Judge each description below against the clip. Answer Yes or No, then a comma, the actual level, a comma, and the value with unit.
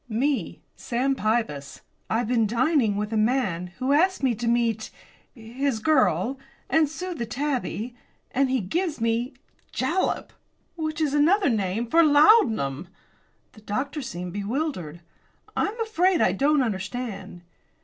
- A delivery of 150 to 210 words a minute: No, average, 140 wpm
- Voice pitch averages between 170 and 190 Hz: No, high, 245 Hz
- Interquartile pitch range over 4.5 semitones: Yes, wide, 5.6 semitones